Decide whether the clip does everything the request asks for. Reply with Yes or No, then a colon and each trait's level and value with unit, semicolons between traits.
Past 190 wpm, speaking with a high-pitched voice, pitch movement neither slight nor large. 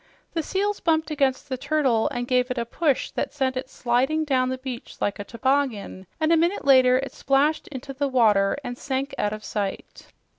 Yes: average, 200 wpm; very high, 265 Hz; average, 3.0 semitones